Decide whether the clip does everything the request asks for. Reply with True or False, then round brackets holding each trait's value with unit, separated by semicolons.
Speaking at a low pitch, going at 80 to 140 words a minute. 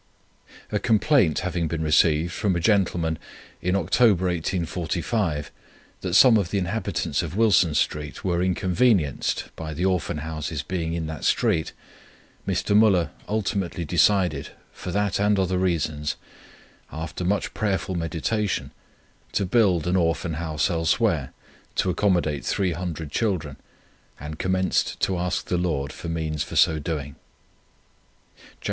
True (85 Hz; 135 wpm)